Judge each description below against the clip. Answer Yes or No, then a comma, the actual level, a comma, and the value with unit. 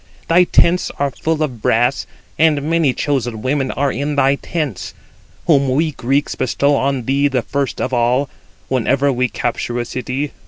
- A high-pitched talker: No, medium, 140 Hz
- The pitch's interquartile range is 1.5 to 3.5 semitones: Yes, narrow, 2.4 semitones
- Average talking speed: Yes, average, 165 wpm